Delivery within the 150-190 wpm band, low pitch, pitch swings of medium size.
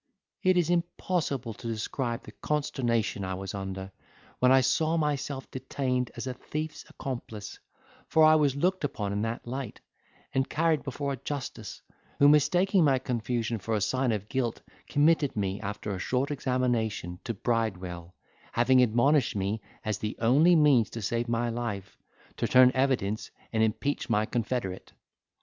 Yes: average, 160 wpm; low, 125 Hz; average, 4.7 semitones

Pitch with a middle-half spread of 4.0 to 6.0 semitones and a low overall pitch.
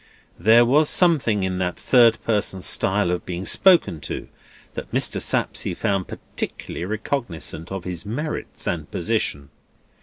Yes: average, 5.0 semitones; low, 100 Hz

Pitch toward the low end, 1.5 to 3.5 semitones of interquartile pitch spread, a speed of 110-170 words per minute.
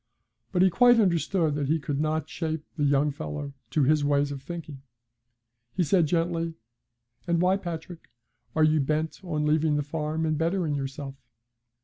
No: medium, 155 Hz; narrow, 2.6 semitones; average, 165 wpm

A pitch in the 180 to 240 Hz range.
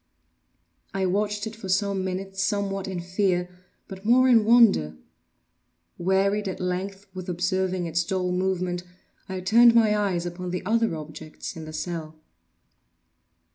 Yes: high, 190 Hz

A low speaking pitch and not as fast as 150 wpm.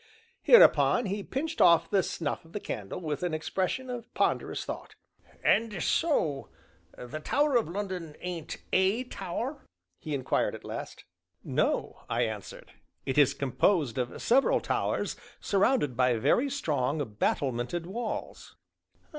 No: medium, 180 Hz; slow, 135 wpm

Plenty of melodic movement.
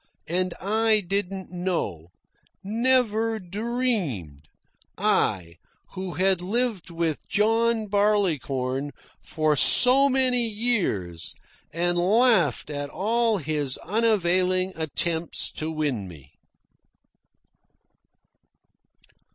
Yes: wide, 6.3 semitones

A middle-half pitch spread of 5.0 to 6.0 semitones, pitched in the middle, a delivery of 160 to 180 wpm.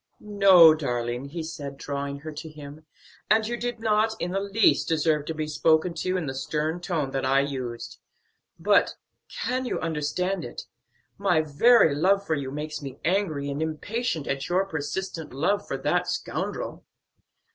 Yes: wide, 5.4 semitones; medium, 160 Hz; average, 170 wpm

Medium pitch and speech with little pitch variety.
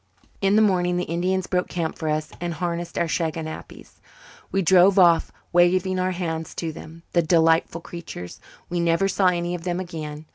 Yes: medium, 175 Hz; narrow, 1.9 semitones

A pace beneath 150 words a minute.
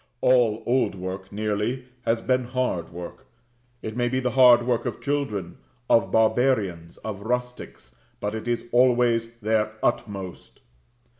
Yes: average, 140 wpm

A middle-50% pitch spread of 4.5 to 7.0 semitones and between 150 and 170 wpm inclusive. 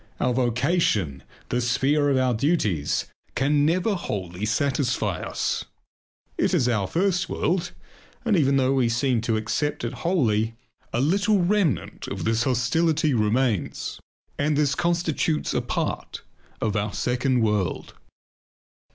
No: wide, 5.6 semitones; slow, 135 wpm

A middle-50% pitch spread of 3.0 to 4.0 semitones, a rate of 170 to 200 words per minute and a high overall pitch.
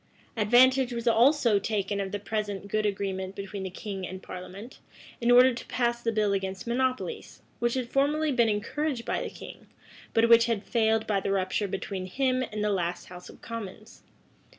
Yes: average, 3.5 semitones; average, 185 wpm; high, 215 Hz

